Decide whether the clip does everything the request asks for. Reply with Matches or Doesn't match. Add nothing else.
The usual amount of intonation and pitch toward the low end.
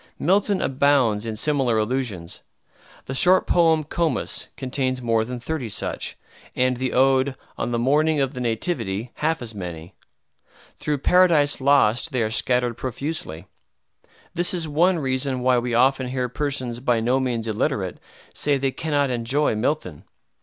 Matches